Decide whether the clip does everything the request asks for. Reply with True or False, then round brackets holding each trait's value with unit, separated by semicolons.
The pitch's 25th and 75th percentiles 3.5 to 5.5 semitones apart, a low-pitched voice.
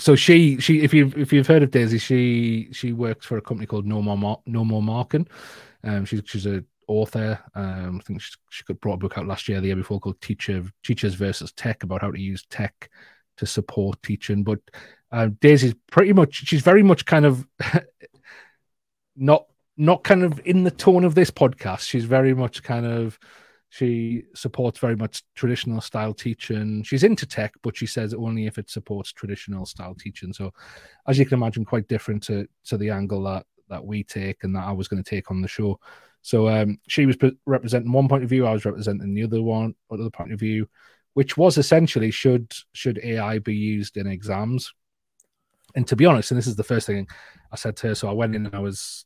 True (4.2 semitones; 110 Hz)